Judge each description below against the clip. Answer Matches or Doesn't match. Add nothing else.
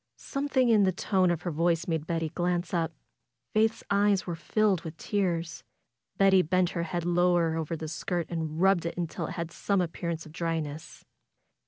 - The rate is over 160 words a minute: Matches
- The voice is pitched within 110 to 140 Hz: Doesn't match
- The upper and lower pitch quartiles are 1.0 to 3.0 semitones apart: Matches